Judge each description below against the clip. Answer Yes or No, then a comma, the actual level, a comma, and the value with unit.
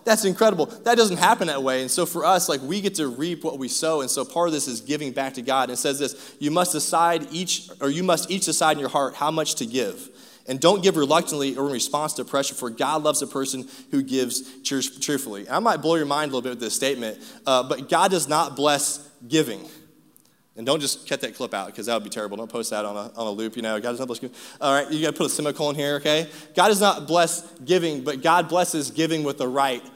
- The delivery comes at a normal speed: No, fast, 265 wpm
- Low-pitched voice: No, medium, 145 Hz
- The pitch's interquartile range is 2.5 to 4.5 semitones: Yes, average, 3.7 semitones